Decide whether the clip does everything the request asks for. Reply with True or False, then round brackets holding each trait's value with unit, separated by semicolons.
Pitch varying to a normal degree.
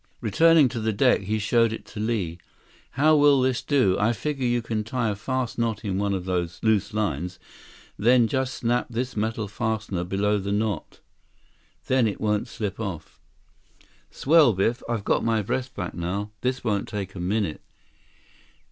True (3.4 semitones)